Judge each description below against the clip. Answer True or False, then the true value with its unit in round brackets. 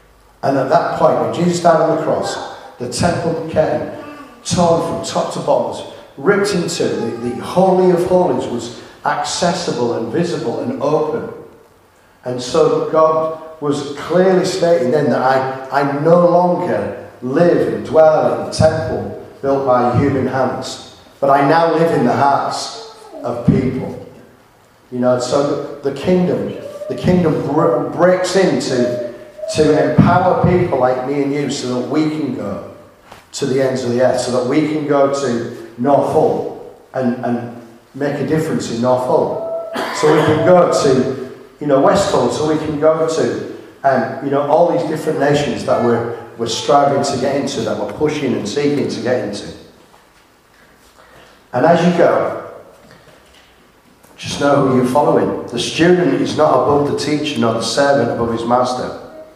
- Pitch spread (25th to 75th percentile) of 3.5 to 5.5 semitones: True (4.6 semitones)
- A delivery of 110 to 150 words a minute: False (165 wpm)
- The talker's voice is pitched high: False (145 Hz)